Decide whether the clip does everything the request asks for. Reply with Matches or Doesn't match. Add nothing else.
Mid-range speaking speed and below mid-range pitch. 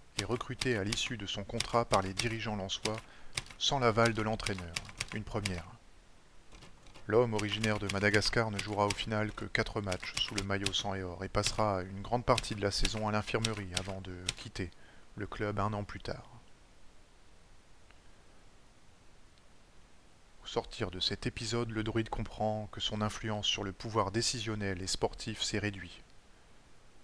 Matches